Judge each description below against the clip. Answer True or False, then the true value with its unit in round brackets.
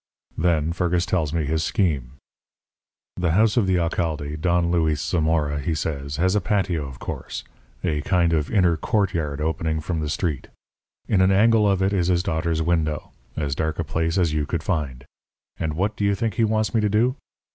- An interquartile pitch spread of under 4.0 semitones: True (3.4 semitones)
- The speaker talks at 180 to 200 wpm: True (195 wpm)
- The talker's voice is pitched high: False (85 Hz)